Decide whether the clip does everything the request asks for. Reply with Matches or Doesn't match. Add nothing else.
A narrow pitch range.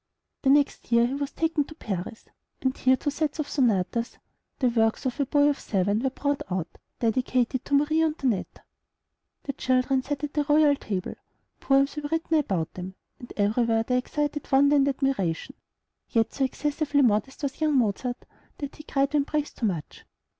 Doesn't match